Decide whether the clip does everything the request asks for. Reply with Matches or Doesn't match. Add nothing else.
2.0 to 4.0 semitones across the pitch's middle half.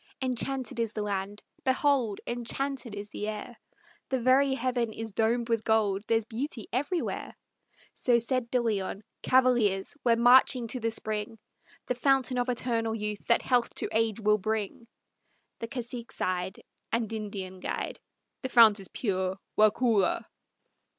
Matches